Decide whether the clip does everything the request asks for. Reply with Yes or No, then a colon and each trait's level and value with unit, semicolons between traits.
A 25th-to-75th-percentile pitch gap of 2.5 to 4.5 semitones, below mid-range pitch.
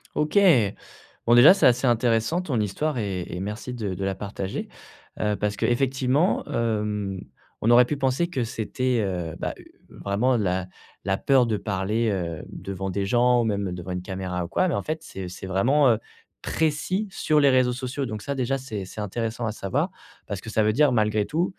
No: average, 5.0 semitones; low, 115 Hz